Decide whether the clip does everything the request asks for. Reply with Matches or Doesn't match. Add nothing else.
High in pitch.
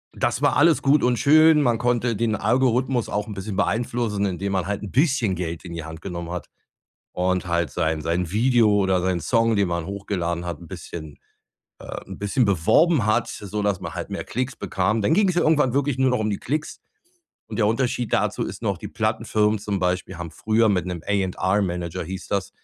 Doesn't match